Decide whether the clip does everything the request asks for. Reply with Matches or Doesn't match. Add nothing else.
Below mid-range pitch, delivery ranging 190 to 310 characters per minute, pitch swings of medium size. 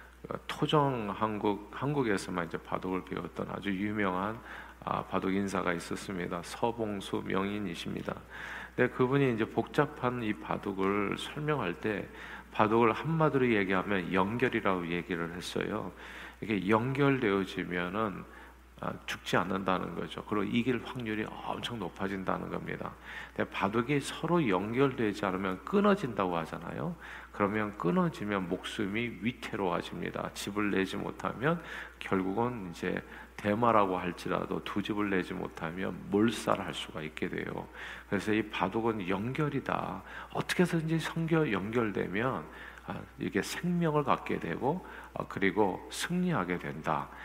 Matches